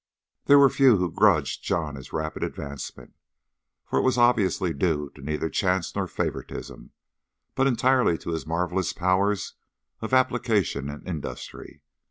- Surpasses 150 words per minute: No, average, 145 wpm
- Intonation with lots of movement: Yes, wide, 7.4 semitones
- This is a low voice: Yes, very low, 90 Hz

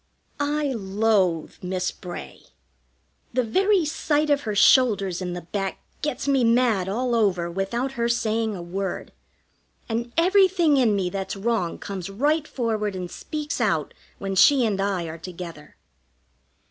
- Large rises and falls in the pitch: Yes, wide, 5.7 semitones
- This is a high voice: Yes, high, 215 Hz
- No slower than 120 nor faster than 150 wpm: Yes, average, 145 wpm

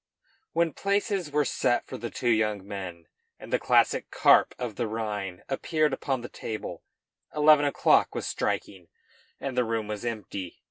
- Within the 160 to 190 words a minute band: Yes, average, 165 wpm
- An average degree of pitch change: No, wide, 5.9 semitones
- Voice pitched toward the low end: Yes, low, 115 Hz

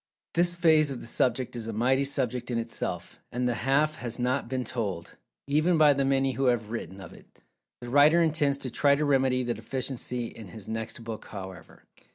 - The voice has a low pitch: Yes, low, 125 Hz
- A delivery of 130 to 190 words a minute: No, fast, 205 wpm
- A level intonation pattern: No, average, 3.4 semitones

